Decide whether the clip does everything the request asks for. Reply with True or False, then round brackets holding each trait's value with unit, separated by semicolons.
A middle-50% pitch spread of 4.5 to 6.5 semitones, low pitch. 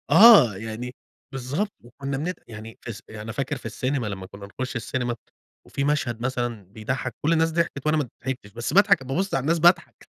True (5.1 semitones; 130 Hz)